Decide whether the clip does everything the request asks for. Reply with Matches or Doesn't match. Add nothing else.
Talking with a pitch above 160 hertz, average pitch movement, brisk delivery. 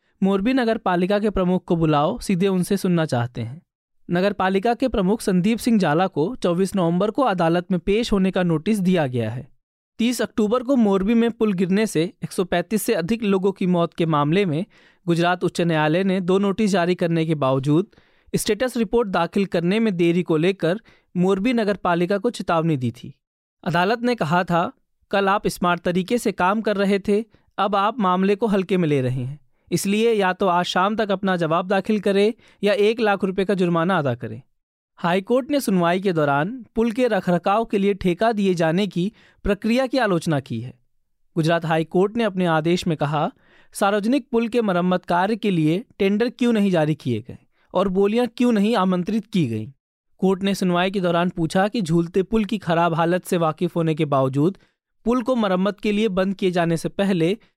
Matches